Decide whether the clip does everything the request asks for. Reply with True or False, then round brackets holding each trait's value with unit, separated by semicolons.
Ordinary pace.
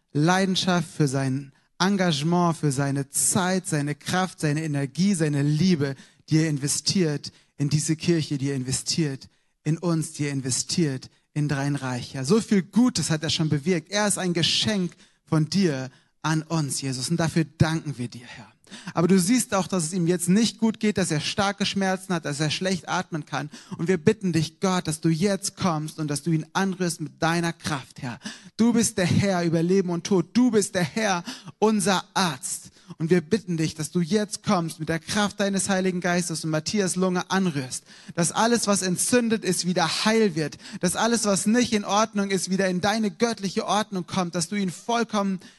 False (195 wpm)